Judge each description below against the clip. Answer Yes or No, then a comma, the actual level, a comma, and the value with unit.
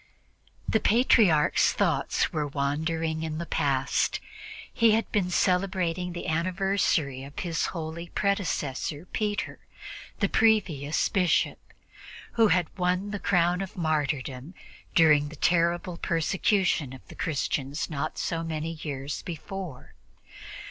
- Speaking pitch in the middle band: Yes, medium, 165 Hz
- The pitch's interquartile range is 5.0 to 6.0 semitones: No, average, 3.8 semitones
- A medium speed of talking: No, slow, 120 wpm